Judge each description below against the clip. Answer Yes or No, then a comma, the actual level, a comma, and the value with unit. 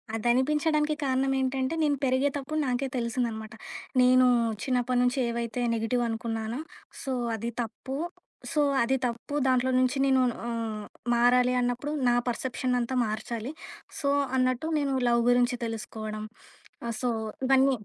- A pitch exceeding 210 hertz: Yes, very high, 250 Hz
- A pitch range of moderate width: No, narrow, 2.1 semitones